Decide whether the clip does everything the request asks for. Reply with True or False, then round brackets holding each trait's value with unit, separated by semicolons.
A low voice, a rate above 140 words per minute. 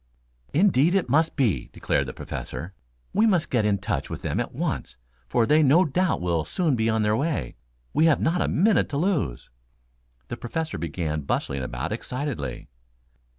True (130 Hz; 175 wpm)